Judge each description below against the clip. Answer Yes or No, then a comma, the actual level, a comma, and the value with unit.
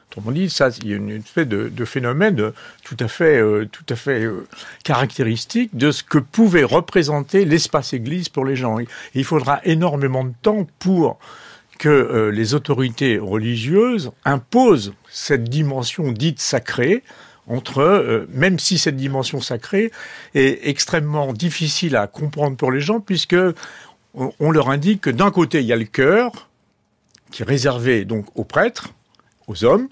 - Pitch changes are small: No, wide, 5.6 semitones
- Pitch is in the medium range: Yes, medium, 145 Hz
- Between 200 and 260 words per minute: No, average, 160 wpm